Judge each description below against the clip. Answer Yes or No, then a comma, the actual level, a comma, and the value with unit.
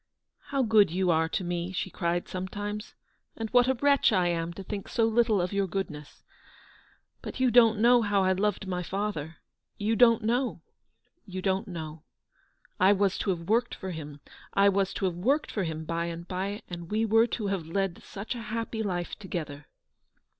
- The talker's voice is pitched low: No, high, 195 Hz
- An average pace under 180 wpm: No, fast, 205 wpm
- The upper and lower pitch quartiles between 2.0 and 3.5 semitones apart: No, average, 4.1 semitones